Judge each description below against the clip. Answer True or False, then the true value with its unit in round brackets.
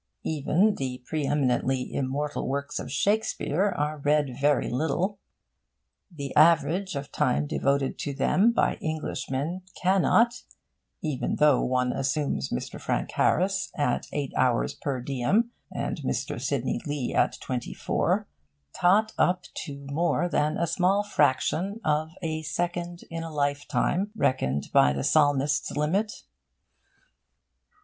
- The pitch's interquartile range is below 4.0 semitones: False (4.3 semitones)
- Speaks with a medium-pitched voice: True (150 Hz)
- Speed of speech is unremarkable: False (130 wpm)